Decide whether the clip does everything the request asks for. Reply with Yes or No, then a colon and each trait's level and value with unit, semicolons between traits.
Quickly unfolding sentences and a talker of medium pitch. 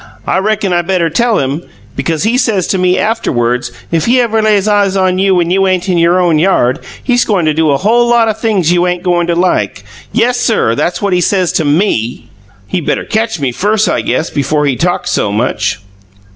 Yes: fast, 220 wpm; medium, 180 Hz